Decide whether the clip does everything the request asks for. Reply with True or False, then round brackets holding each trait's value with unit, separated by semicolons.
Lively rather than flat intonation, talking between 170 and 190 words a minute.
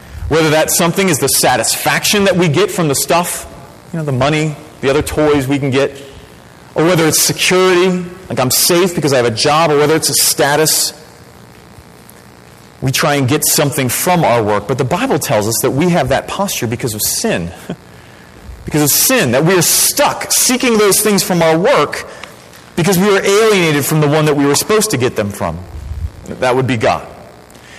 False (8.1 semitones; 200 wpm)